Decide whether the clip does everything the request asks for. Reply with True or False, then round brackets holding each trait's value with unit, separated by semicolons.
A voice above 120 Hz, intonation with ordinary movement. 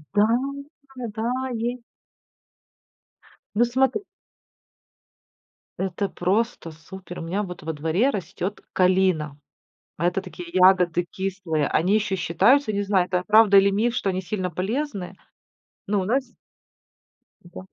True (190 Hz; 3.2 semitones)